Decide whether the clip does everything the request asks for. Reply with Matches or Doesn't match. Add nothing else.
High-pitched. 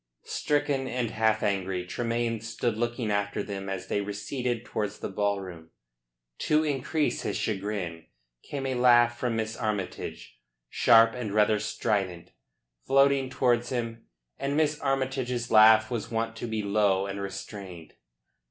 Doesn't match